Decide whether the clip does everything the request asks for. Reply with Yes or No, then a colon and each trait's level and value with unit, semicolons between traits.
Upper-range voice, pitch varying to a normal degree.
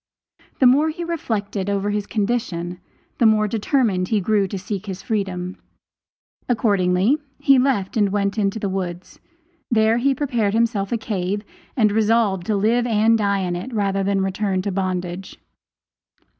Yes: high, 205 Hz; average, 3.0 semitones